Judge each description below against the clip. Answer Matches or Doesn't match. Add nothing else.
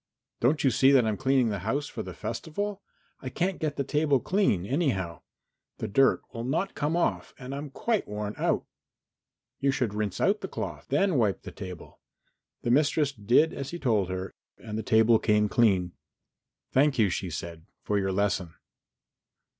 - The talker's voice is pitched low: Matches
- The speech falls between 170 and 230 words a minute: Matches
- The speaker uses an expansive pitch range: Matches